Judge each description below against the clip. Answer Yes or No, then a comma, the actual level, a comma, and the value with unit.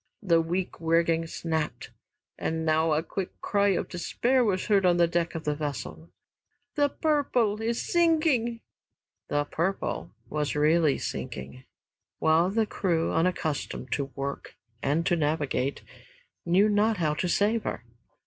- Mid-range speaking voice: Yes, medium, 170 Hz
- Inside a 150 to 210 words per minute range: No, average, 140 wpm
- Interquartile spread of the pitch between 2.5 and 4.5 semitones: No, average, 5.1 semitones